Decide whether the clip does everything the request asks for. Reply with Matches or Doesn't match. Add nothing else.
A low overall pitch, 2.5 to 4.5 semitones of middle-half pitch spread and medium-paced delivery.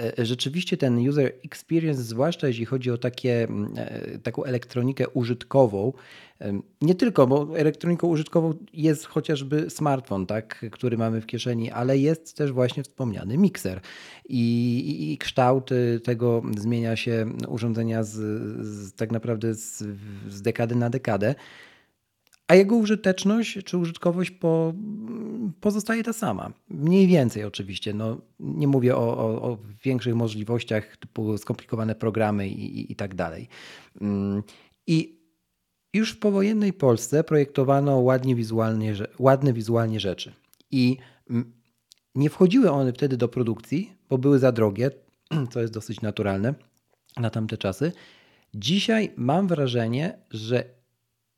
Doesn't match